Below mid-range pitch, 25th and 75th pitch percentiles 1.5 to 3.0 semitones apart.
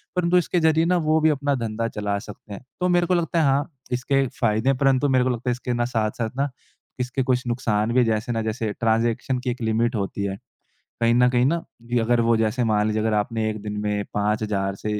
No: low, 120 Hz; average, 3.8 semitones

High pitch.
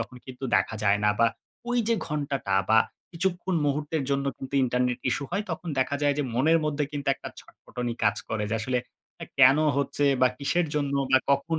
No: medium, 140 Hz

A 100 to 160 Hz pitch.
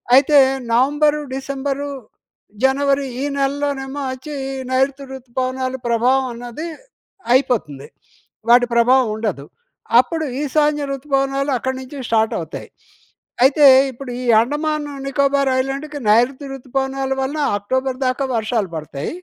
No: very high, 265 Hz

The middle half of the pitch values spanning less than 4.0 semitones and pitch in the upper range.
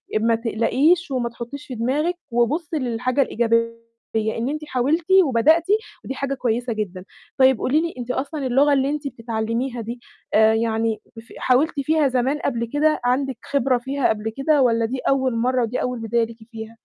Yes: average, 3.4 semitones; very high, 250 Hz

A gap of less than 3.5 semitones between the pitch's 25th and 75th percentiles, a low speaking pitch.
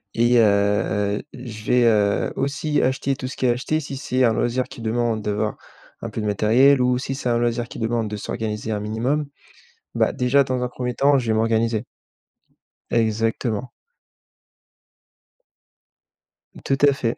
Yes: average, 2.8 semitones; low, 120 Hz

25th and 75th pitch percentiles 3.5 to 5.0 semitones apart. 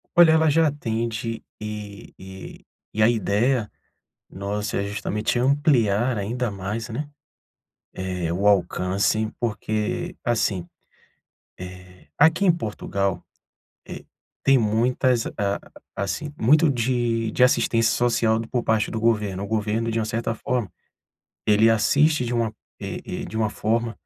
No: average, 3.0 semitones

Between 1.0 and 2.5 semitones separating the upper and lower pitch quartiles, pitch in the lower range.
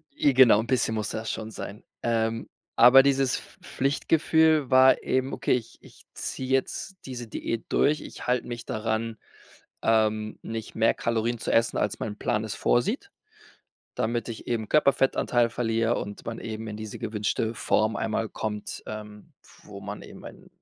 No: average, 2.9 semitones; low, 115 Hz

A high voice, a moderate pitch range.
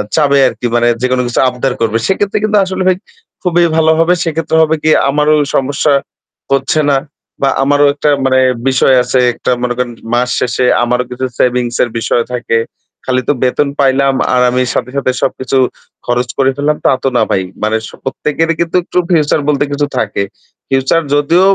No: low, 135 Hz; average, 3.4 semitones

